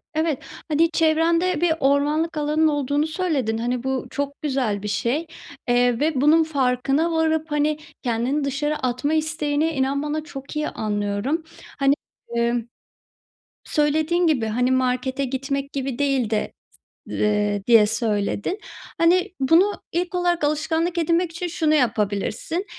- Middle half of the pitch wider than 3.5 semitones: Yes, average, 4.2 semitones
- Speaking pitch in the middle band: No, very high, 290 Hz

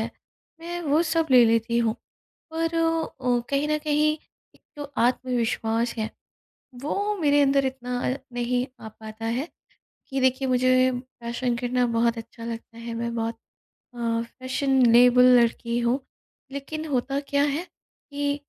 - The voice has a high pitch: Yes, very high, 255 Hz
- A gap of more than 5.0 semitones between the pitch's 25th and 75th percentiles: No, average, 3.4 semitones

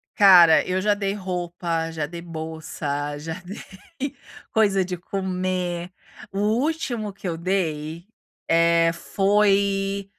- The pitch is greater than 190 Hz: No, medium, 185 Hz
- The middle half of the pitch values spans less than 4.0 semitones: Yes, average, 3.1 semitones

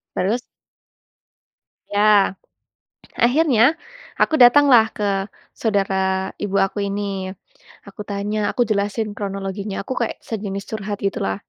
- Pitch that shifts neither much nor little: No, narrow, 2.2 semitones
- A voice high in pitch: Yes, high, 205 Hz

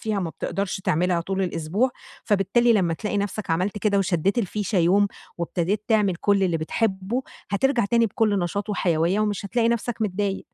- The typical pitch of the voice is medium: No, high, 200 Hz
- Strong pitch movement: No, average, 2.9 semitones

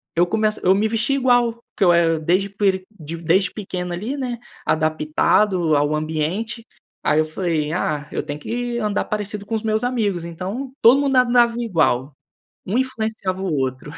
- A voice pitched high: Yes, high, 195 Hz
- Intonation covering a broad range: Yes, wide, 5.8 semitones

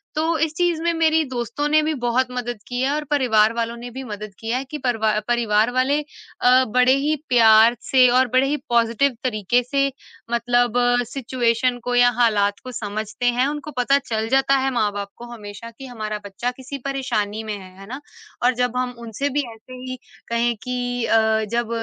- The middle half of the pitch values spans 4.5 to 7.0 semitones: No, average, 2.9 semitones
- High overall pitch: Yes, high, 245 Hz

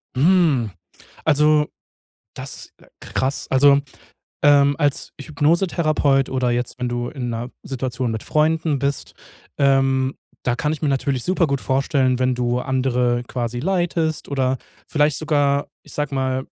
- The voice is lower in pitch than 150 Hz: Yes, low, 135 Hz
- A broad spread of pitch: No, average, 2.7 semitones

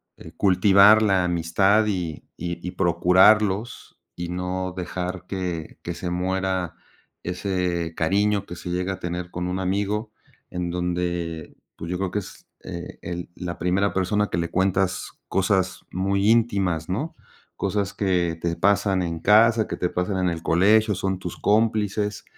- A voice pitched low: Yes, very low, 95 Hz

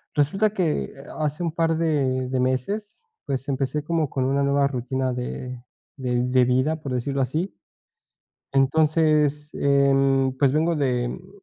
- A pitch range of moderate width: Yes, average, 3.2 semitones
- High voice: No, medium, 140 Hz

